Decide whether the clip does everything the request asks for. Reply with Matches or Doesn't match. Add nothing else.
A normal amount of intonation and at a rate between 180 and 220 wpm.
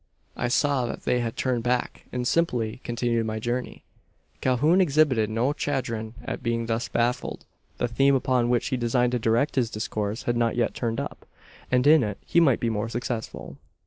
Doesn't match